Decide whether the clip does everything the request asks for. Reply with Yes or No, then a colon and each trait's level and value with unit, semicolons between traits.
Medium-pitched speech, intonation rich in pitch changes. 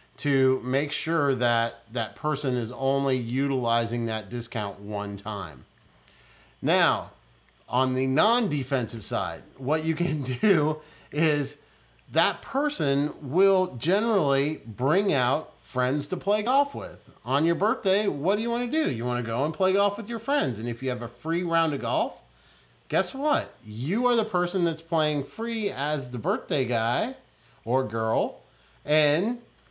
Yes: medium, 145 Hz; wide, 7.5 semitones